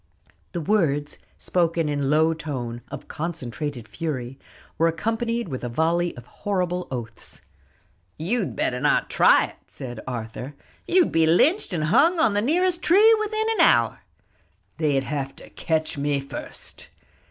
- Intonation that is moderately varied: No, wide, 7.1 semitones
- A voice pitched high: No, medium, 160 Hz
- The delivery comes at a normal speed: Yes, average, 145 wpm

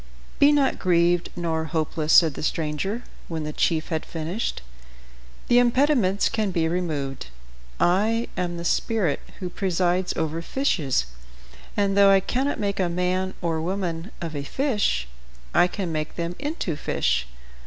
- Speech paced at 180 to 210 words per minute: No, average, 150 wpm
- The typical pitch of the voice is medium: Yes, medium, 175 Hz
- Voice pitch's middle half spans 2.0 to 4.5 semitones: Yes, average, 3.9 semitones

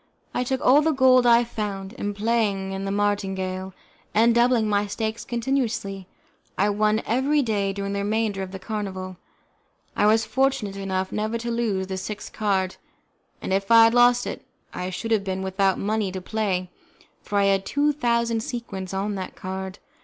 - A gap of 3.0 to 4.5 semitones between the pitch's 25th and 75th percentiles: Yes, average, 3.3 semitones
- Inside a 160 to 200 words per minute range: Yes, average, 175 wpm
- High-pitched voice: Yes, high, 205 Hz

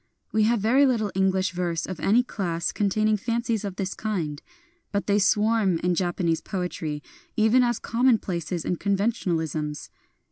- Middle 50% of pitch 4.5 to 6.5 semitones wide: No, average, 3.9 semitones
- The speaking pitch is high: Yes, high, 195 Hz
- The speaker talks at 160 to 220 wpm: No, average, 150 wpm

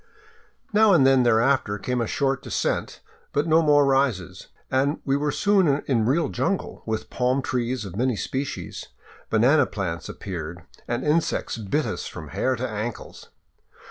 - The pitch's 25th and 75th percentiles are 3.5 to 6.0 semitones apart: Yes, average, 4.3 semitones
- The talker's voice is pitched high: No, low, 130 Hz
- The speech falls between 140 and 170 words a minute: Yes, average, 155 wpm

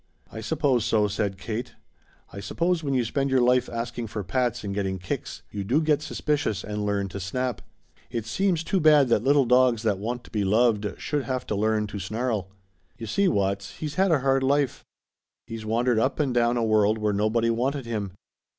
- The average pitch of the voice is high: No, low, 115 Hz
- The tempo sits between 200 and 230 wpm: Yes, fast, 205 wpm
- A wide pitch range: No, average, 4.2 semitones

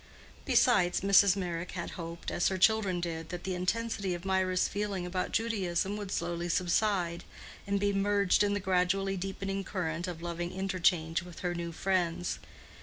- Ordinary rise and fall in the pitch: No, narrow, 2.1 semitones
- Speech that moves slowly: No, average, 165 wpm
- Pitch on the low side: No, medium, 185 Hz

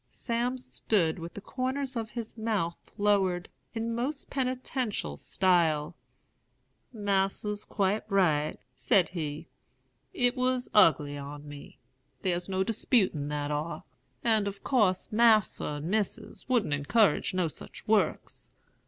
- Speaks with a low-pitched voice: No, high, 200 Hz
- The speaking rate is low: Yes, slow, 125 wpm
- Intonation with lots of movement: Yes, wide, 5.9 semitones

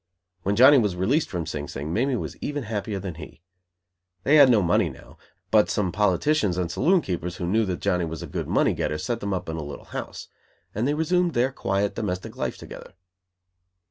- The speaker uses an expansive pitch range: Yes, wide, 6.3 semitones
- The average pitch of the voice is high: No, low, 100 Hz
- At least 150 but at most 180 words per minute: No, fast, 205 wpm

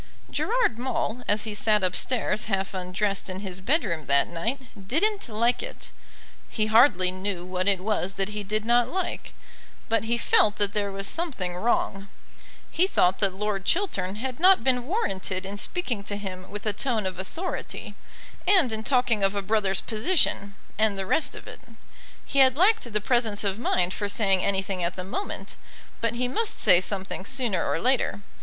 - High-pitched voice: Yes, high, 210 Hz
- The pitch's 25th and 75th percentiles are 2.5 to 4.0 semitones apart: No, average, 4.4 semitones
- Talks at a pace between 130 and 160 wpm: No, average, 180 wpm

